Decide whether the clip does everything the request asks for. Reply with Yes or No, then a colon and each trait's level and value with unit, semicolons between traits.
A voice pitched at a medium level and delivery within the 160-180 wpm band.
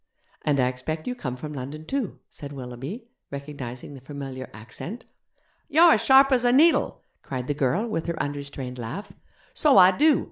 Yes: medium, 145 Hz; average, 175 wpm